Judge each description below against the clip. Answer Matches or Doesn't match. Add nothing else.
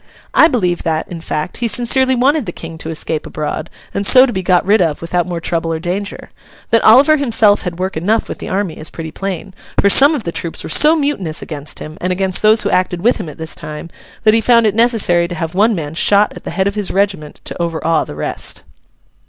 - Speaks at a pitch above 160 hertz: Matches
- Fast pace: Matches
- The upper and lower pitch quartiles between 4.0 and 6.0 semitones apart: Matches